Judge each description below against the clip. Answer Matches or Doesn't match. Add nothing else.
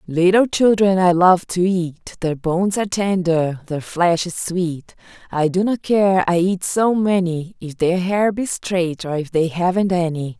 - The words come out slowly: Doesn't match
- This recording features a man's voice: Doesn't match